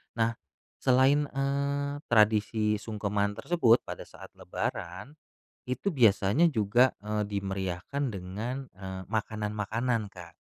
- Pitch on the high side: No, low, 110 Hz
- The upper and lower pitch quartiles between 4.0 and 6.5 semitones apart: Yes, average, 4.5 semitones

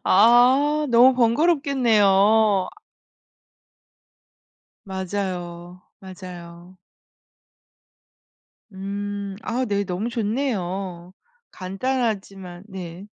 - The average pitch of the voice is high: Yes, high, 200 Hz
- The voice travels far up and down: No, average, 4.7 semitones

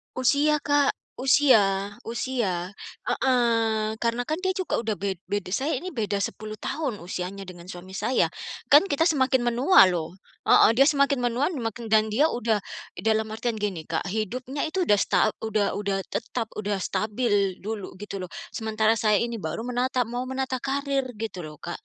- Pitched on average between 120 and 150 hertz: No, high, 225 Hz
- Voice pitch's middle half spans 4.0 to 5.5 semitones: Yes, average, 4.4 semitones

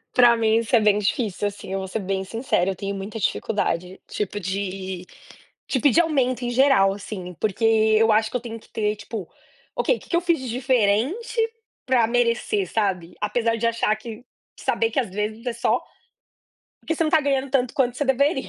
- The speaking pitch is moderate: No, high, 225 Hz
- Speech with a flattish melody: No, average, 4.0 semitones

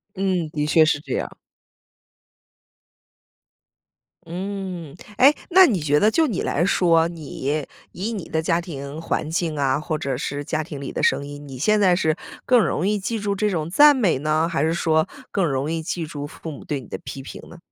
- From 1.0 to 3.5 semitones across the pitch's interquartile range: No, average, 4.4 semitones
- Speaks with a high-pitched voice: No, medium, 165 Hz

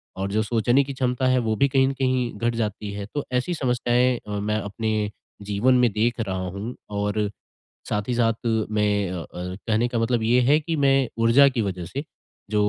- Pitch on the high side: No, low, 115 Hz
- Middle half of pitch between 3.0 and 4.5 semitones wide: Yes, average, 3.5 semitones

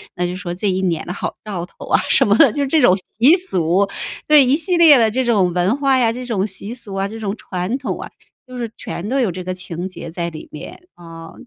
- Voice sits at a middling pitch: No, high, 200 Hz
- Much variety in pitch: Yes, wide, 5.9 semitones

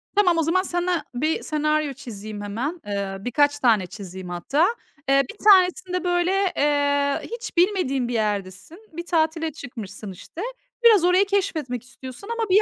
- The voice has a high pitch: Yes, very high, 295 Hz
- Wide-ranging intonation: Yes, wide, 7.3 semitones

